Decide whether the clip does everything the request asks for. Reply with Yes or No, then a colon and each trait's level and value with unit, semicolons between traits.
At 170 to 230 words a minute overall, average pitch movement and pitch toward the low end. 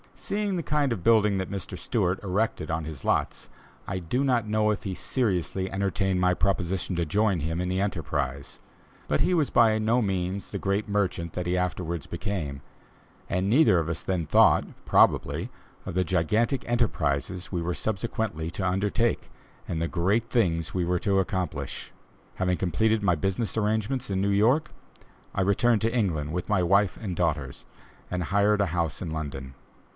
Yes: average, 175 wpm; average, 3.9 semitones; very low, 95 Hz